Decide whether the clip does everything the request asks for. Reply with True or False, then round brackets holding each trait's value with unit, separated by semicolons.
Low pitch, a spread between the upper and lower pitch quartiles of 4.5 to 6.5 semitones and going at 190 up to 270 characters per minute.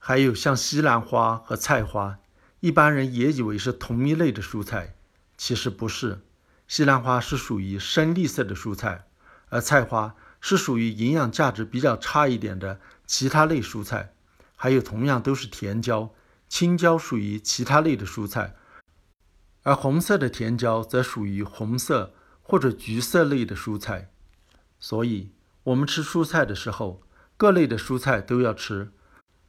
True (115 Hz; 5.0 semitones; 230 characters per minute)